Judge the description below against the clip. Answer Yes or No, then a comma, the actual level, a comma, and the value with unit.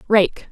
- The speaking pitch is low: No, high, 190 Hz